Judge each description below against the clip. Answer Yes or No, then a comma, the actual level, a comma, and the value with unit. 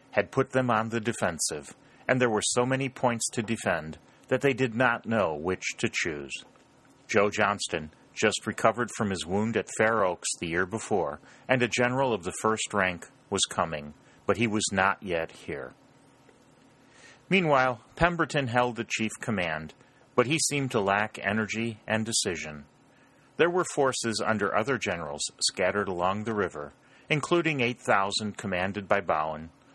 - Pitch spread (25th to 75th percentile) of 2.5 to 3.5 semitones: No, average, 4.5 semitones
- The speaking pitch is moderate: No, low, 110 Hz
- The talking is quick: No, average, 160 wpm